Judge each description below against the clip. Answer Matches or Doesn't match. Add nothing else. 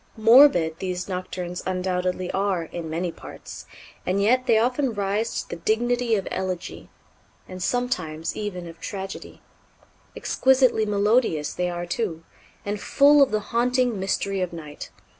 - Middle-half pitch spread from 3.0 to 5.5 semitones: Matches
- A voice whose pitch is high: Matches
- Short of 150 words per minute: Matches